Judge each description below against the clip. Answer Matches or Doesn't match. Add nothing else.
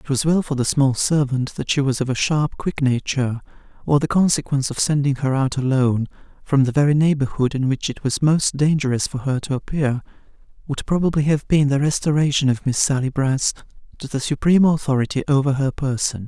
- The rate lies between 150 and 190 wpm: Doesn't match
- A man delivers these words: Matches